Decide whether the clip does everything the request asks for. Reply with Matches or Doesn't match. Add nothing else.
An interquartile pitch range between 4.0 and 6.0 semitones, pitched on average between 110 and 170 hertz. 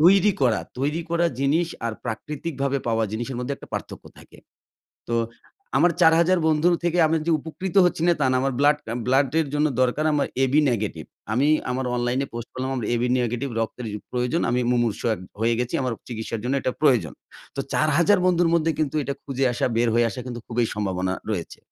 Matches